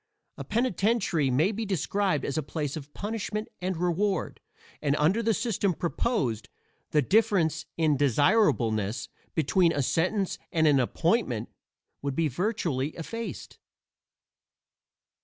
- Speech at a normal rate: No, slow, 120 wpm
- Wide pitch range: Yes, wide, 6.2 semitones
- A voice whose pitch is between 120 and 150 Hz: No, medium, 165 Hz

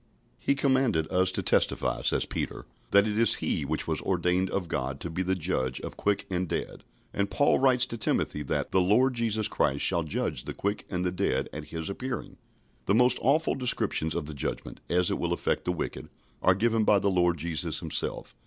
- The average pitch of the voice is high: No, very low, 95 Hz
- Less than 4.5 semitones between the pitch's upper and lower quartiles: No, average, 4.9 semitones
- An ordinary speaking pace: No, fast, 210 wpm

